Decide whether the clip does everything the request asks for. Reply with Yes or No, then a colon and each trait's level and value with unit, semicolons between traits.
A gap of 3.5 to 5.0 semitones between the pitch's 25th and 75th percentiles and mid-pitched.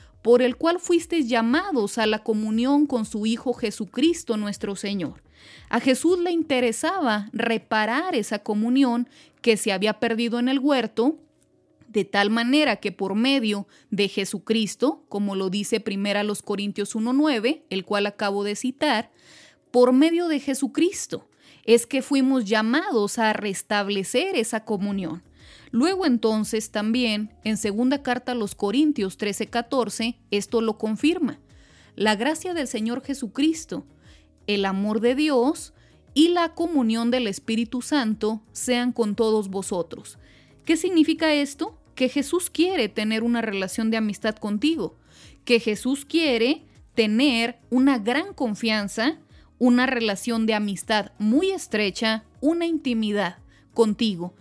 No: average, 4.4 semitones; high, 235 Hz